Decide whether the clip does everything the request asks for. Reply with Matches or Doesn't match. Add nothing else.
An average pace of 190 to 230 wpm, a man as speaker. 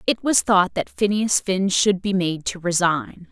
Doesn't match